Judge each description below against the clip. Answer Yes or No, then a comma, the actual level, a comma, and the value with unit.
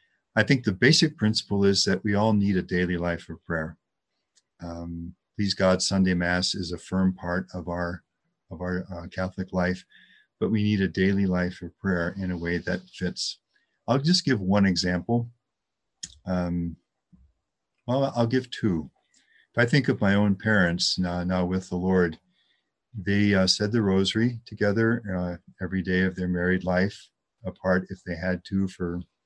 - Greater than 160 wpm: Yes, average, 175 wpm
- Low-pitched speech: Yes, very low, 95 Hz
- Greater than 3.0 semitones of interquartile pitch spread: No, narrow, 2.6 semitones